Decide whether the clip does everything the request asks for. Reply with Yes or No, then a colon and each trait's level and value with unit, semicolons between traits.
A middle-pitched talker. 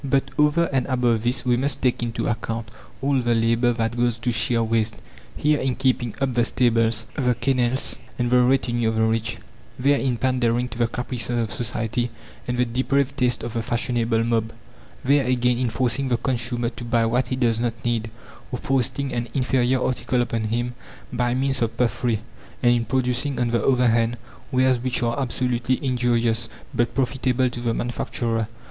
No: low, 120 Hz